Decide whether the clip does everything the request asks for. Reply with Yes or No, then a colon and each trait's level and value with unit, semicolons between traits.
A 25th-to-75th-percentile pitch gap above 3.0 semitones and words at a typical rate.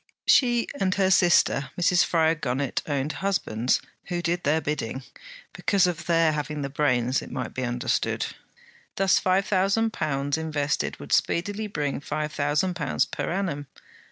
Yes: average, 4.6 semitones; average, 155 wpm